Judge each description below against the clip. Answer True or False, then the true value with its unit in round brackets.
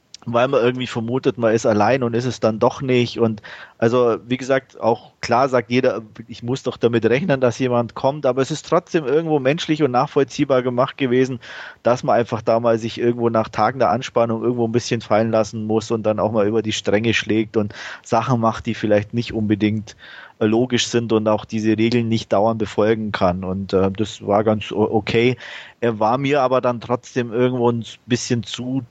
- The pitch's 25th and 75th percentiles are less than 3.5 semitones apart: True (2.4 semitones)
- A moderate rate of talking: False (200 wpm)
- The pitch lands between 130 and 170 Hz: False (115 Hz)